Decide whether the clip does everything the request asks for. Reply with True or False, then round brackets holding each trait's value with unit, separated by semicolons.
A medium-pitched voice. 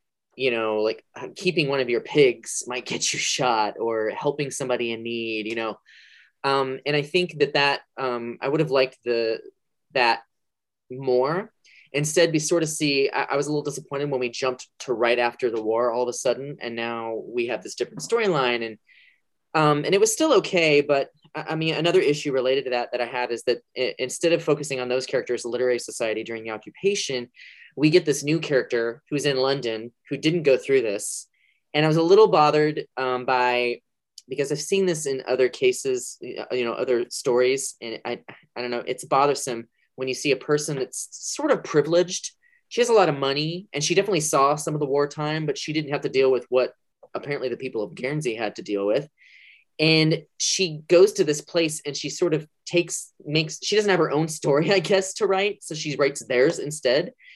True (145 Hz)